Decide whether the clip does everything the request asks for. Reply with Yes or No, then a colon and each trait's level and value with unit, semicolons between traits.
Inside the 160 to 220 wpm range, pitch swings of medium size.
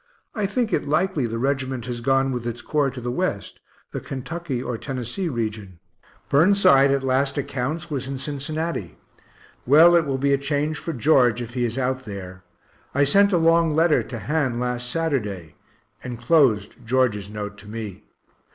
Yes: average, 170 wpm; average, 4.3 semitones